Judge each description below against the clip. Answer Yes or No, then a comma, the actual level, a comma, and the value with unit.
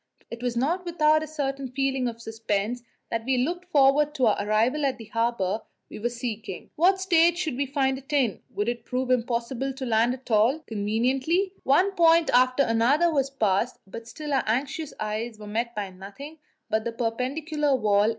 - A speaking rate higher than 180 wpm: Yes, average, 190 wpm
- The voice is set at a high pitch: Yes, very high, 255 Hz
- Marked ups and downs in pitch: No, average, 4.5 semitones